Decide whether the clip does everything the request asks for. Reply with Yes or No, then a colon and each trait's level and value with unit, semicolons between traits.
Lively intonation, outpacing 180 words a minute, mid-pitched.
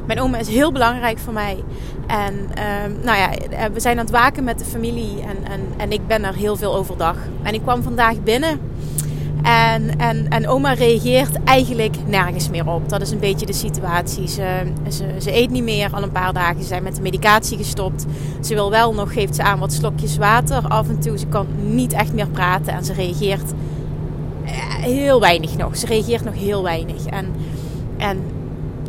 Yes: wide, 6.4 semitones; fast, 200 wpm; medium, 165 Hz